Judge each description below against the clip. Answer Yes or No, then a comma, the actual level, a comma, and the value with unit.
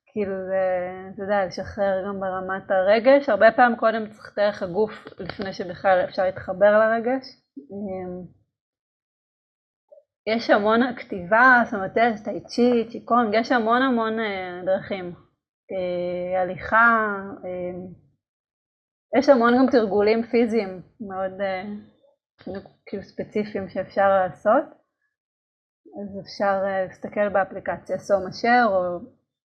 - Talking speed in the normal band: No, slow, 90 wpm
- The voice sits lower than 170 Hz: No, high, 205 Hz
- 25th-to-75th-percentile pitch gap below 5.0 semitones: Yes, average, 3.7 semitones